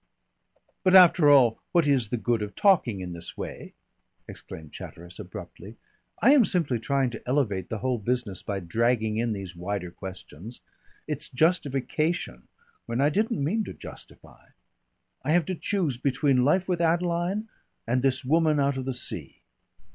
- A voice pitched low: Yes, low, 130 Hz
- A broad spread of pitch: Yes, wide, 6.8 semitones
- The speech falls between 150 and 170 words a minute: Yes, average, 160 wpm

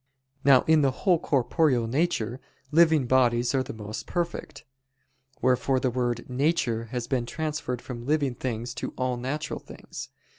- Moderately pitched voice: No, low, 130 Hz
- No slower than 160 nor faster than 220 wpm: No, average, 150 wpm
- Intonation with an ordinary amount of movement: Yes, average, 3.7 semitones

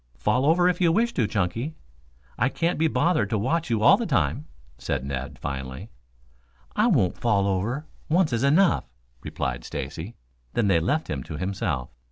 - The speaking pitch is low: Yes, low, 115 Hz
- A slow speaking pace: No, average, 175 wpm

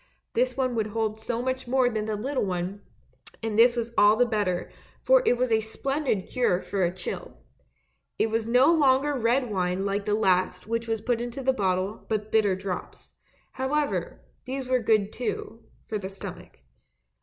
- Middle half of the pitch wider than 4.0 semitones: No, average, 3.7 semitones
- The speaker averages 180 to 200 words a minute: Yes, average, 190 wpm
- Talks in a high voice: Yes, high, 225 Hz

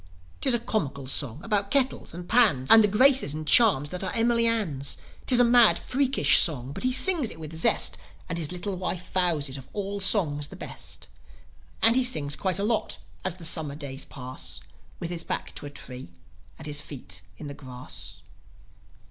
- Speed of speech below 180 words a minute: No, average, 195 wpm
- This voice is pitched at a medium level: Yes, medium, 175 Hz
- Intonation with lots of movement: Yes, wide, 8.0 semitones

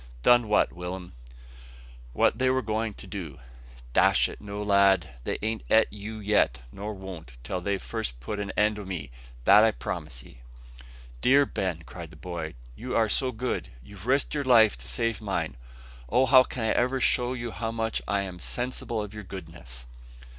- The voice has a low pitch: Yes, low, 105 Hz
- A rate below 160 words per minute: No, average, 185 wpm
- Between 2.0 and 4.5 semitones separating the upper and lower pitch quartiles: Yes, average, 4.2 semitones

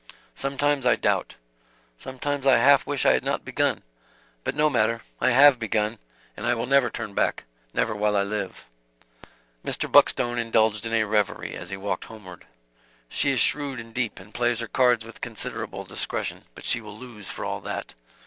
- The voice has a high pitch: No, low, 115 Hz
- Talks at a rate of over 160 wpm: Yes, average, 185 wpm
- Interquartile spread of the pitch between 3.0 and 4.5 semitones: Yes, average, 3.5 semitones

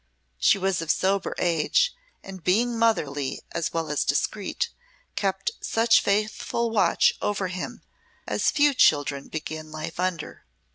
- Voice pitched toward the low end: No, high, 190 Hz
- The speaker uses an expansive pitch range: Yes, wide, 5.9 semitones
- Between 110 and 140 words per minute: Yes, slow, 135 wpm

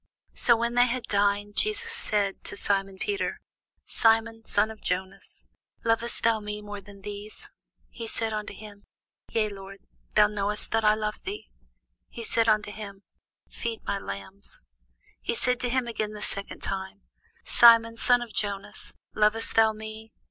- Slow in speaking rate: No, average, 160 wpm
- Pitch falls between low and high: No, high, 215 Hz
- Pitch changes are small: Yes, narrow, 2.1 semitones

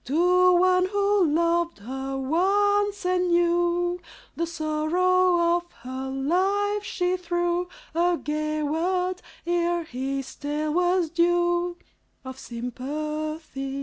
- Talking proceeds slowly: Yes, slow, 110 wpm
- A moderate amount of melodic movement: Yes, average, 3.0 semitones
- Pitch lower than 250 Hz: No, very high, 345 Hz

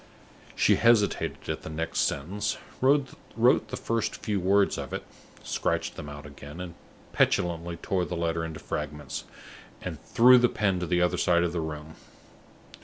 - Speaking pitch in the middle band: No, very low, 85 Hz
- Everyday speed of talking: Yes, average, 165 wpm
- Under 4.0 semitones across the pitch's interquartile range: No, average, 4.4 semitones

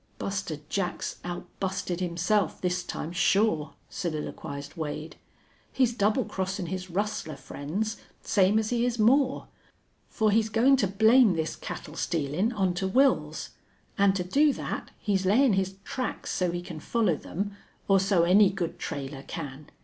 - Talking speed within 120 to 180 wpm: Yes, average, 150 wpm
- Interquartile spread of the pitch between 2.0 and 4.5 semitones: Yes, average, 4.2 semitones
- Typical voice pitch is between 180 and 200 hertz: Yes, high, 190 Hz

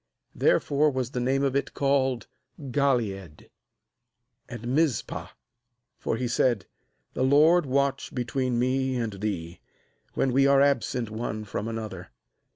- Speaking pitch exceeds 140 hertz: No, low, 130 Hz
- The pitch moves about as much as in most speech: Yes, average, 3.5 semitones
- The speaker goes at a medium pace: No, slow, 130 wpm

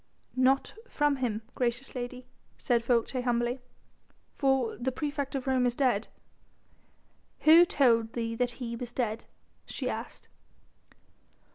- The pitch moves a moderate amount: No, narrow, 2.3 semitones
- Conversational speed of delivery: No, slow, 125 wpm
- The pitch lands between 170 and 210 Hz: No, very high, 250 Hz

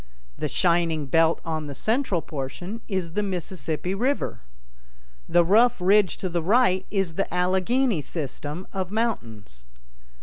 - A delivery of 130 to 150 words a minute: Yes, slow, 135 wpm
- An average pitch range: Yes, average, 4.1 semitones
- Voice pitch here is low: No, medium, 180 Hz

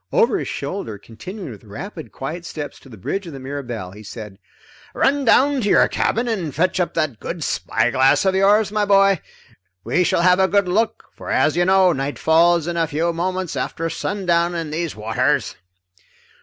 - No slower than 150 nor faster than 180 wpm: No, average, 190 wpm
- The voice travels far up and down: Yes, wide, 6.0 semitones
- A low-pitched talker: No, medium, 170 Hz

